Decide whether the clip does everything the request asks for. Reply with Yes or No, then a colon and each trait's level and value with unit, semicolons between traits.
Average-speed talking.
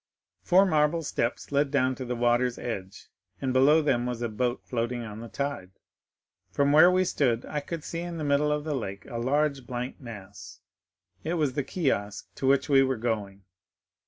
Yes: average, 195 wpm